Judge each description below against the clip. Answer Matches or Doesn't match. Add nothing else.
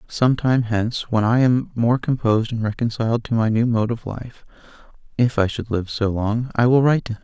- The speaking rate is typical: Doesn't match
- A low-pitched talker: Matches